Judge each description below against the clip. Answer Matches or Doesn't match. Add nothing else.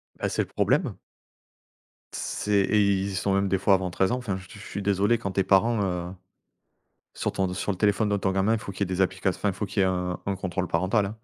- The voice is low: Matches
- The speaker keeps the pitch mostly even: Matches